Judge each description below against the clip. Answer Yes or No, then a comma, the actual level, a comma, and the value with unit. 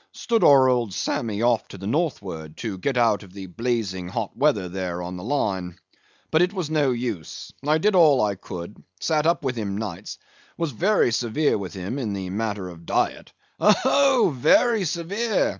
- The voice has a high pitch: No, low, 120 Hz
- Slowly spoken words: No, average, 180 wpm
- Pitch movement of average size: No, wide, 8.4 semitones